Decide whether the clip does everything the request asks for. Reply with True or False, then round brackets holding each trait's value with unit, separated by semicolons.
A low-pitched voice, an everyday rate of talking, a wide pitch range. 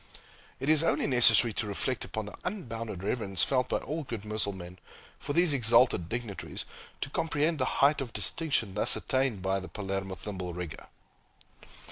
True (115 Hz; 160 wpm; 5.7 semitones)